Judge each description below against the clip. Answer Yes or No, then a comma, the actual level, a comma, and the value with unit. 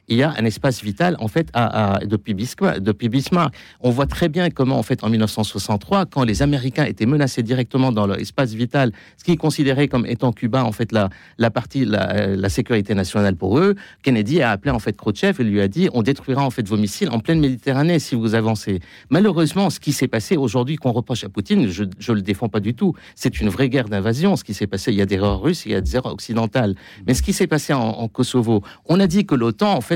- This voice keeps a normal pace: No, fast, 250 wpm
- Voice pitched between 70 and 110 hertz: No, low, 120 Hz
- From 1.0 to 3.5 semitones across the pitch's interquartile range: No, average, 5.0 semitones